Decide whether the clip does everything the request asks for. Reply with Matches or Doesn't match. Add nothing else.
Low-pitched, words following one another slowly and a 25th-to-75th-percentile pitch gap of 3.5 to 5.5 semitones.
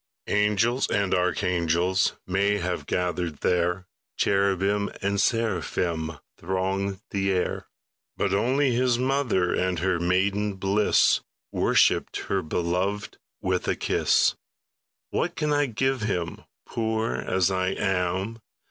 Doesn't match